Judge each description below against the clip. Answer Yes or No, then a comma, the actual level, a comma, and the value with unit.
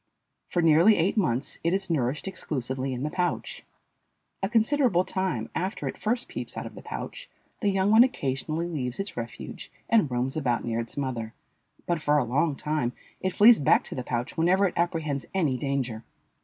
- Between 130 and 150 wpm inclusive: No, average, 185 wpm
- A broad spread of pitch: Yes, wide, 6.6 semitones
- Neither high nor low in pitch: Yes, medium, 155 Hz